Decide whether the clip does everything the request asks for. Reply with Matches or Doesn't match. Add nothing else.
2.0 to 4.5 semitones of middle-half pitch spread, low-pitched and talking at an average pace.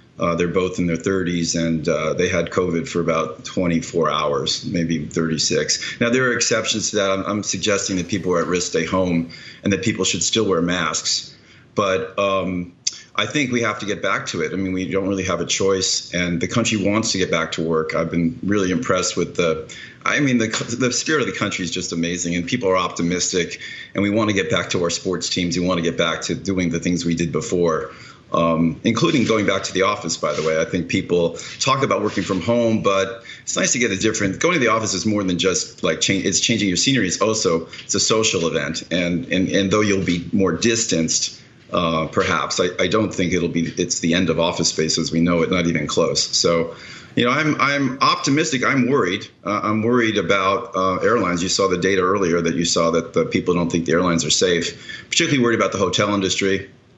Doesn't match